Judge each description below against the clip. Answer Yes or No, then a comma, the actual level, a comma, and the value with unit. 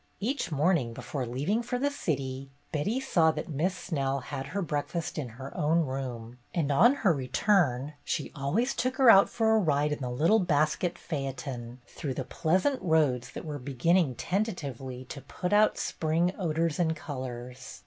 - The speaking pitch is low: No, medium, 150 Hz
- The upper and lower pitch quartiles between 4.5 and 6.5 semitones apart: Yes, wide, 5.6 semitones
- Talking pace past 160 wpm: Yes, average, 170 wpm